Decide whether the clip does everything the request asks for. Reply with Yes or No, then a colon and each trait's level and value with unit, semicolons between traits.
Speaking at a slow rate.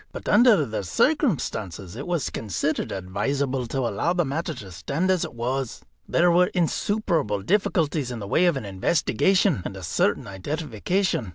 No: average, 165 wpm